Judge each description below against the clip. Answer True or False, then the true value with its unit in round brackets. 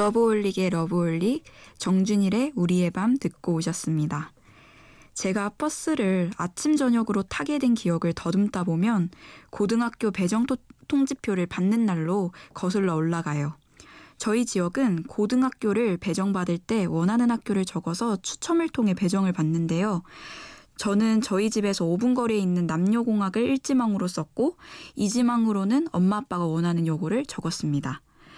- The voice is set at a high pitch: True (200 Hz)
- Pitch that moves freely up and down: False (5.0 semitones)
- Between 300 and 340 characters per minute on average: True (315 characters per minute)